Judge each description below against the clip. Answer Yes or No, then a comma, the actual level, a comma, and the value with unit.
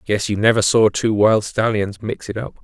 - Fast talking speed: Yes, fast, 230 wpm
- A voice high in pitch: No, low, 105 Hz